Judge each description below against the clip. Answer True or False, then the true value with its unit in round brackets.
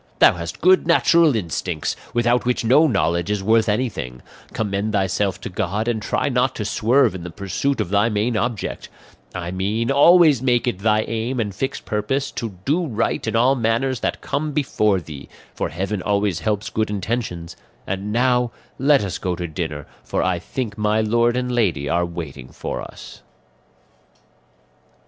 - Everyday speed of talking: True (170 wpm)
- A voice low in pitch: True (110 Hz)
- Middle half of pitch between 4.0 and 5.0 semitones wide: True (4.7 semitones)